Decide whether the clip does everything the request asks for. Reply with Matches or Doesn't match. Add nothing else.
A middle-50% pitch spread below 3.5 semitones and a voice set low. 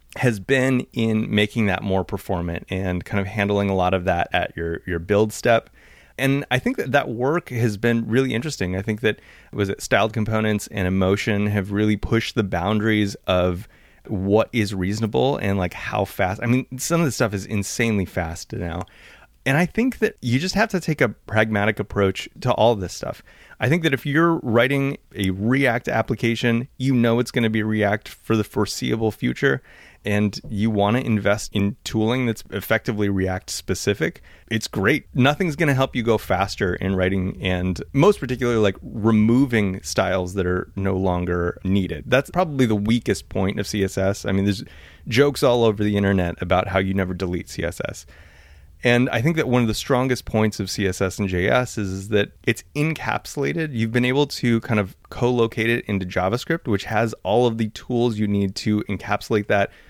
Doesn't match